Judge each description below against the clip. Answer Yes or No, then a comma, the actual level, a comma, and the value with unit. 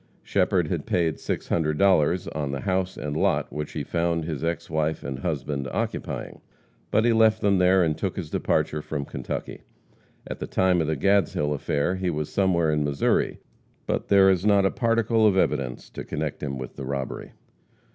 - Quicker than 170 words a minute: Yes, average, 185 wpm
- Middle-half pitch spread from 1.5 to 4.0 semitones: No, average, 4.5 semitones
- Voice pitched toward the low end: Yes, very low, 85 Hz